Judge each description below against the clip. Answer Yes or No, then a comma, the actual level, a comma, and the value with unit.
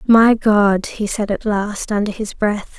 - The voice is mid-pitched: No, high, 210 Hz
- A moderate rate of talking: Yes, average, 195 wpm